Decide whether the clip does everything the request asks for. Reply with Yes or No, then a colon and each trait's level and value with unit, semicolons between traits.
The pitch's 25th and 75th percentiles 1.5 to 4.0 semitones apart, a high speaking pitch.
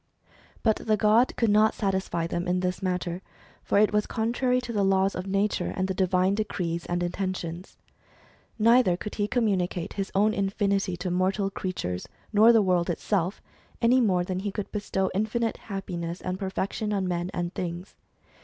Yes: narrow, 2.6 semitones; high, 195 Hz